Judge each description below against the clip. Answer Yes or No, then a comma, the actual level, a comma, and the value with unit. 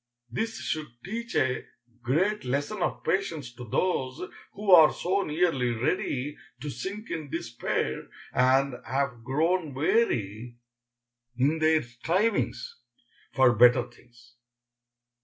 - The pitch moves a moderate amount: No, wide, 6.5 semitones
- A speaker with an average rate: No, slow, 115 wpm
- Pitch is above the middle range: No, medium, 140 Hz